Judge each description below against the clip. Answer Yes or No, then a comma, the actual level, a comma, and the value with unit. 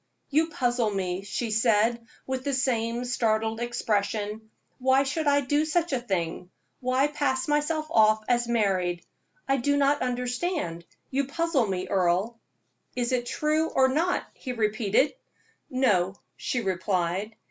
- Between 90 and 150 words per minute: Yes, average, 140 wpm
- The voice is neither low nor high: No, high, 240 Hz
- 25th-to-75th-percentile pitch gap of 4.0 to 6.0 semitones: Yes, average, 4.6 semitones